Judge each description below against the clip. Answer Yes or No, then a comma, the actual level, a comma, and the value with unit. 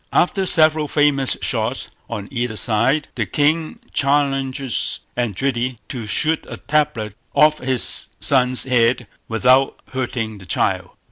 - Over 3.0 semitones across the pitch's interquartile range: Yes, average, 3.8 semitones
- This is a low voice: Yes, low, 130 Hz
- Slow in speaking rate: Yes, slow, 125 wpm